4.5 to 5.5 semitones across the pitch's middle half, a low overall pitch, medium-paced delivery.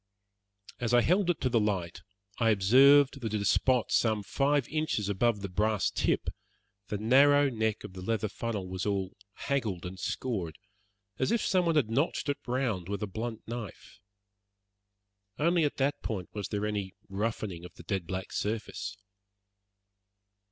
Yes: average, 5.1 semitones; low, 110 Hz; average, 165 wpm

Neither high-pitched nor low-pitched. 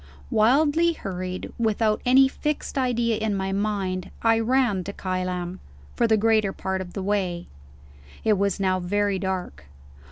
No: high, 205 Hz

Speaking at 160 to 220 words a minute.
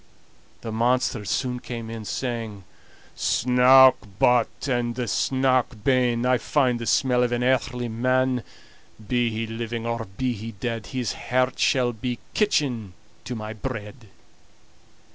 No: slow, 135 wpm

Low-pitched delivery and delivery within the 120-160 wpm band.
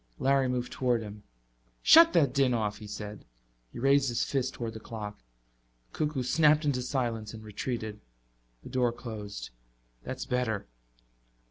Yes: low, 120 Hz; average, 150 wpm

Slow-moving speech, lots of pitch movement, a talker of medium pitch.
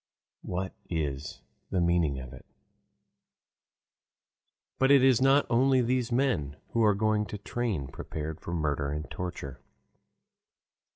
No: slow, 125 wpm; wide, 8.4 semitones; very low, 90 Hz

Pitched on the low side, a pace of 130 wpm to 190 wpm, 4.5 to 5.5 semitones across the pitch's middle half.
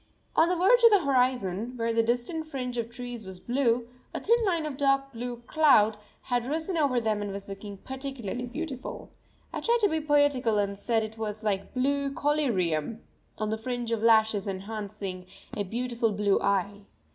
No: high, 240 Hz; average, 180 wpm; average, 4.8 semitones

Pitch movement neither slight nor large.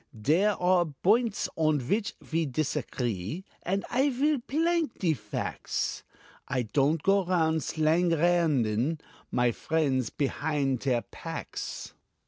No: wide, 5.9 semitones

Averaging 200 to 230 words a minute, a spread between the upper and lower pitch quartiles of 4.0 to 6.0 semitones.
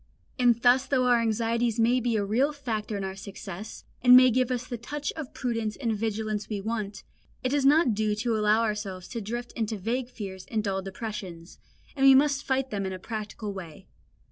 No: fast, 205 wpm; average, 3.3 semitones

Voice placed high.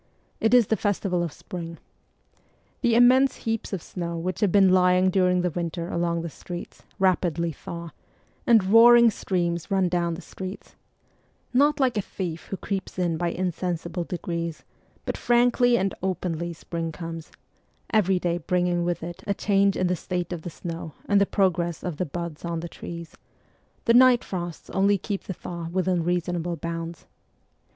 No: medium, 180 Hz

